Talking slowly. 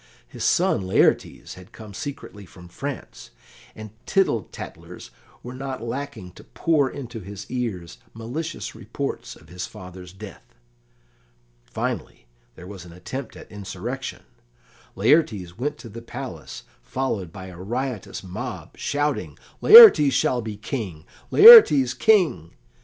Yes: slow, 130 wpm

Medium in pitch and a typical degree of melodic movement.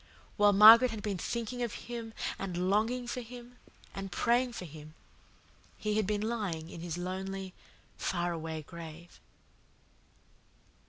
No: high, 200 Hz; average, 4.9 semitones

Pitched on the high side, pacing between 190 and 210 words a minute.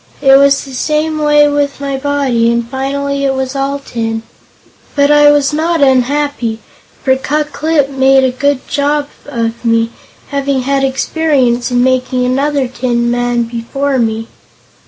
No: very high, 270 Hz; average, 155 wpm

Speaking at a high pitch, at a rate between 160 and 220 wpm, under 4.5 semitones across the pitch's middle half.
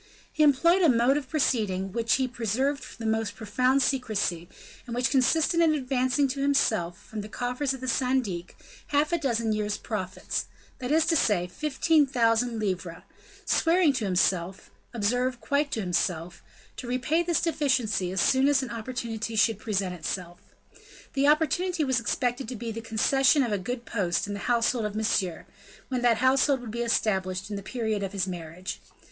No: high, 235 Hz; average, 180 wpm; average, 4.8 semitones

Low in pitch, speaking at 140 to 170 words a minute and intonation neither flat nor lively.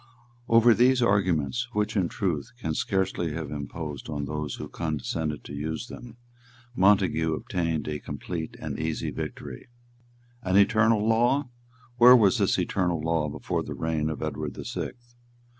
No: very low, 85 Hz; average, 150 wpm; wide, 6.3 semitones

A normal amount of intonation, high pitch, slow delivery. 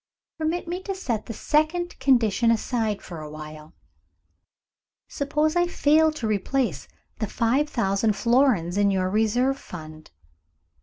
No: wide, 7.4 semitones; high, 230 Hz; slow, 125 wpm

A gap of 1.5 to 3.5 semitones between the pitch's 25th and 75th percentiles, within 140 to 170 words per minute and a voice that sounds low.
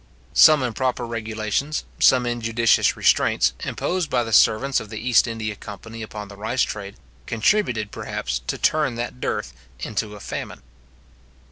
Yes: average, 2.7 semitones; average, 145 wpm; low, 115 Hz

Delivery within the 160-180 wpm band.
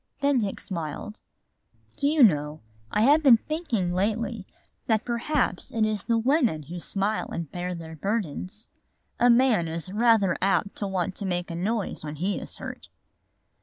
Yes: average, 165 wpm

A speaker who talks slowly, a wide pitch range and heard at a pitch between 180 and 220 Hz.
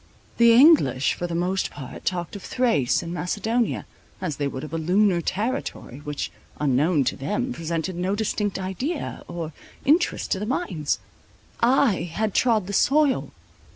No: average, 155 wpm; wide, 6.1 semitones; medium, 185 Hz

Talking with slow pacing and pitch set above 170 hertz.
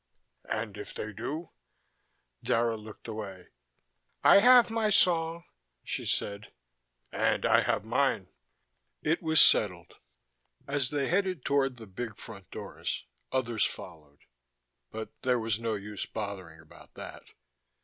No: slow, 130 wpm; low, 115 Hz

